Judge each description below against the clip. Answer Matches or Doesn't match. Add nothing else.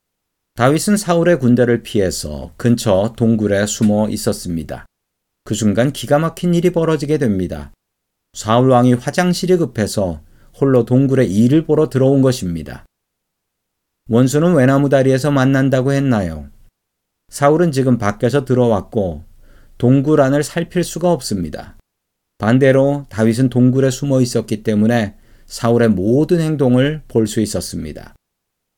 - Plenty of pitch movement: Doesn't match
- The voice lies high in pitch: Doesn't match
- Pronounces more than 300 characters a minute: Doesn't match